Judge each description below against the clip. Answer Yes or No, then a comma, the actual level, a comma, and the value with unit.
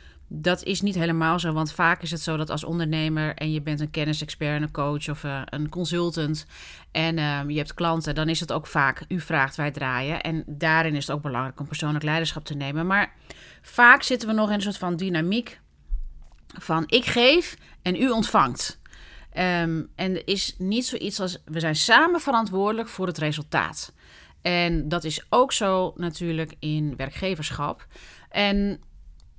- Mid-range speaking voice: Yes, medium, 160 Hz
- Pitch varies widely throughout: No, average, 3.7 semitones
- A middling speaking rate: Yes, average, 180 wpm